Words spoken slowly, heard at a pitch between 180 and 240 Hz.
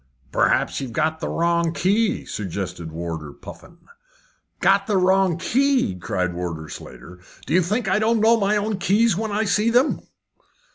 No: average, 160 wpm; medium, 185 Hz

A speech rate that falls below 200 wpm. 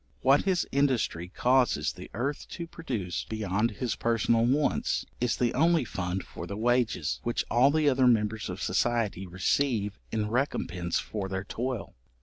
Yes: average, 155 wpm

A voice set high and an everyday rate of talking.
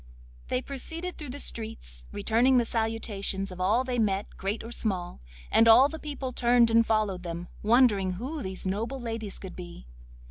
Yes: high, 225 Hz; average, 175 wpm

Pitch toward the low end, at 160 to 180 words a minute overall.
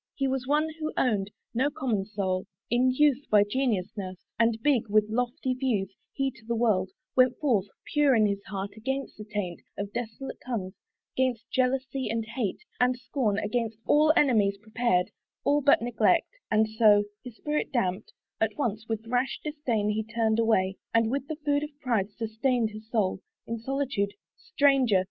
No: high, 230 Hz; average, 170 wpm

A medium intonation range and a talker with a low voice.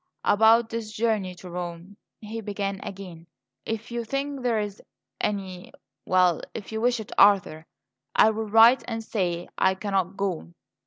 No: average, 3.3 semitones; high, 205 Hz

